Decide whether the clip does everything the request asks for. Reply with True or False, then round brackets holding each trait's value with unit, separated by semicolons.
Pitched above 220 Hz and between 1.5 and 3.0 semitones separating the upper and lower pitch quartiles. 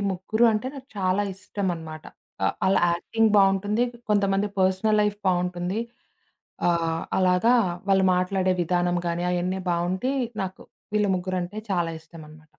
False (185 Hz; 2.5 semitones)